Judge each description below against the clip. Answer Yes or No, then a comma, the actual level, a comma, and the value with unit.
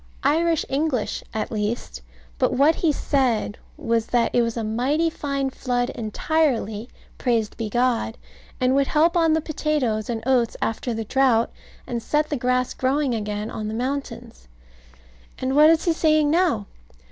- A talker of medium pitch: No, very high, 255 Hz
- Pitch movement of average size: Yes, average, 4.9 semitones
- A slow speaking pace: No, average, 160 wpm